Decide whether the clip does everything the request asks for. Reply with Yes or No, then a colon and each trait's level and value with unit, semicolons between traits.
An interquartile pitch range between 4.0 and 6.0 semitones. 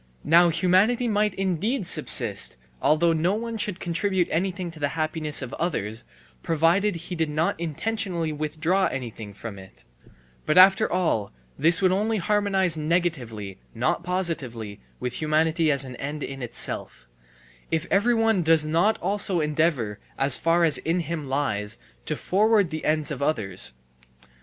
Yes: average, 4.4 semitones